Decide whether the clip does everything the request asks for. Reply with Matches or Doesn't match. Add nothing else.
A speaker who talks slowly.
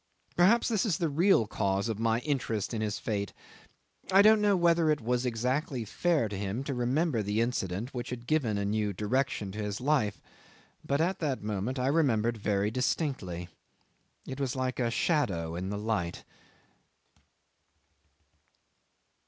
Doesn't match